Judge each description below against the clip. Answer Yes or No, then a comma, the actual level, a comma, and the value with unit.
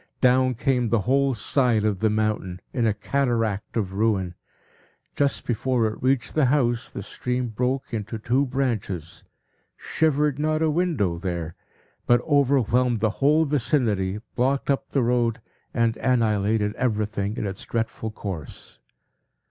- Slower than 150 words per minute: Yes, average, 140 wpm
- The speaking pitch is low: Yes, low, 120 Hz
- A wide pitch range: No, average, 3.9 semitones